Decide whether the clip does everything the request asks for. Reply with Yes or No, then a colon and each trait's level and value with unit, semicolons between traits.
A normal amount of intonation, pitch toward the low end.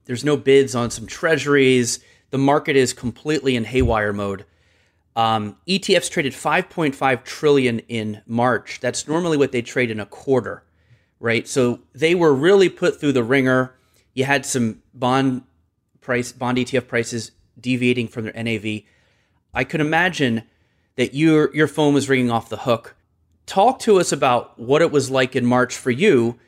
Yes: average, 3.5 semitones; low, 125 Hz